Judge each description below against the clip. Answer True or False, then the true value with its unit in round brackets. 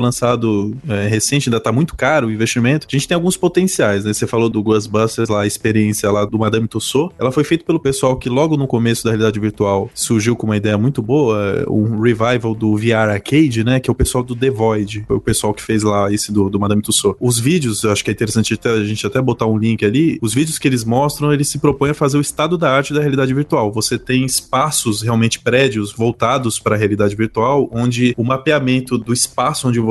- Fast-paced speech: True (235 wpm)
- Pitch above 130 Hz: False (115 Hz)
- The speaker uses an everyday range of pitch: True (3.8 semitones)